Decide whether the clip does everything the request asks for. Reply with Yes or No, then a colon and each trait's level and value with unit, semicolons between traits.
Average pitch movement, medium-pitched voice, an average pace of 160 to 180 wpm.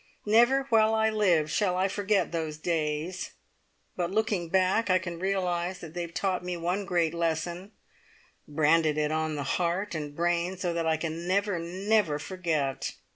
Yes: average, 3.1 semitones; medium, 175 Hz; average, 165 wpm